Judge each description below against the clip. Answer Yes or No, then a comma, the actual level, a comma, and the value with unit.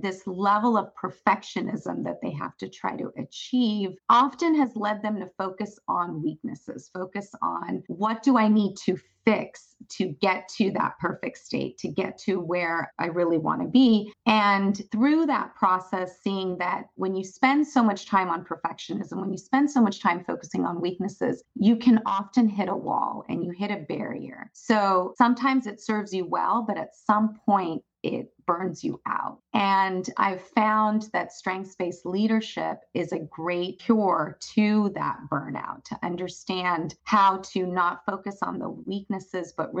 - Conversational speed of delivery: Yes, average, 175 wpm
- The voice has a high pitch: Yes, high, 200 Hz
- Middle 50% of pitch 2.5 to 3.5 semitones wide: Yes, average, 2.8 semitones